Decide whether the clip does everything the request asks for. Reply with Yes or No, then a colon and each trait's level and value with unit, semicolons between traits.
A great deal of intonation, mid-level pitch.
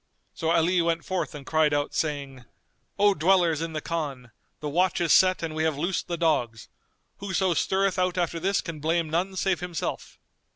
No: average, 3.0 semitones; medium, 165 Hz